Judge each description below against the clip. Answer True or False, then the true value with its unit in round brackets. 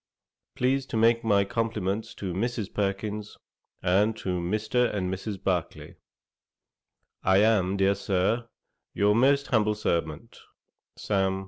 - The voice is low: True (105 Hz)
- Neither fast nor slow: False (120 wpm)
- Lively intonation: False (2.9 semitones)